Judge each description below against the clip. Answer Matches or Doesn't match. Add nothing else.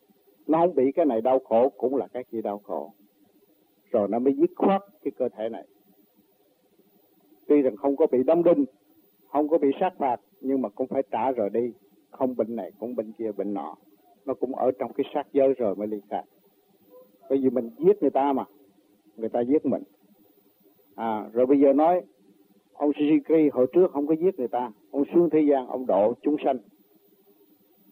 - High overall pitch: Doesn't match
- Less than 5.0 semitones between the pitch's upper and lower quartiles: Doesn't match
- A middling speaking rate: Matches